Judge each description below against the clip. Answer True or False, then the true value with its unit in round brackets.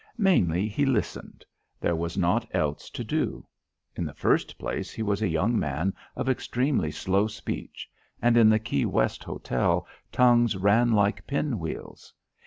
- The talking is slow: False (160 wpm)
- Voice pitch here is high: False (105 Hz)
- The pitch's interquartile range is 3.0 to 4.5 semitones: False (5.6 semitones)